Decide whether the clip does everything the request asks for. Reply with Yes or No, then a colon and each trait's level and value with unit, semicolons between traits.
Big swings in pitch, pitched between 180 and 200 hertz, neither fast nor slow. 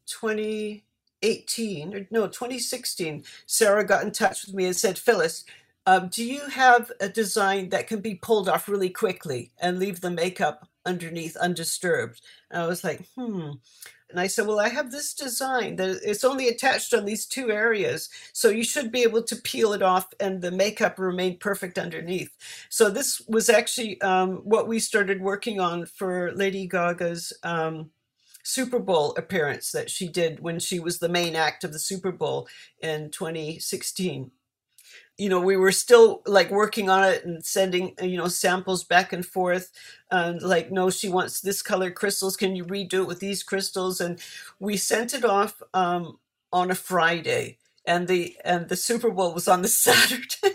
No: average, 3.8 semitones; high, 190 Hz; average, 180 wpm